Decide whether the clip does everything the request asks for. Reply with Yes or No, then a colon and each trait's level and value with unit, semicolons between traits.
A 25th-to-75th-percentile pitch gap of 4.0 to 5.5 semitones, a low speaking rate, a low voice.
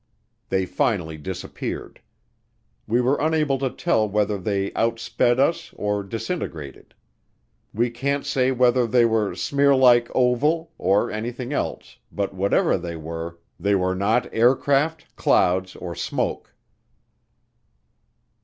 Yes: average, 5.2 semitones; slow, 115 wpm; low, 115 Hz